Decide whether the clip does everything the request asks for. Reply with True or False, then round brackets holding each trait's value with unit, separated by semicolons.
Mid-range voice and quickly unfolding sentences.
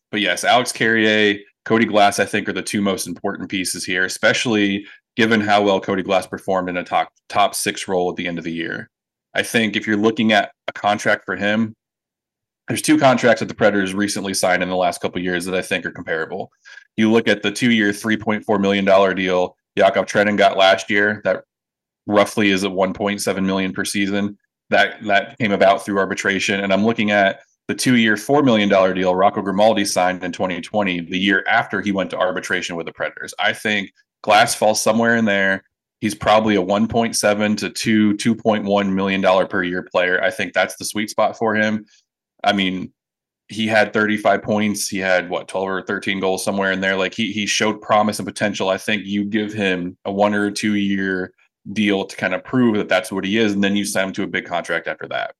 False (100 Hz; 210 wpm)